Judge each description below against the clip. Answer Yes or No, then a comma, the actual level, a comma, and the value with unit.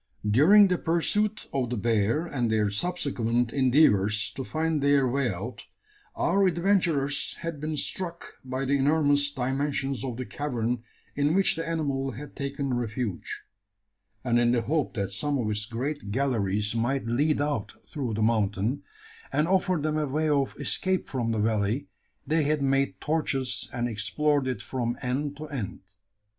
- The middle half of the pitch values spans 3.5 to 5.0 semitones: Yes, average, 4.4 semitones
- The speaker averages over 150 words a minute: Yes, average, 160 wpm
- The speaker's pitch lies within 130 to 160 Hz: Yes, low, 135 Hz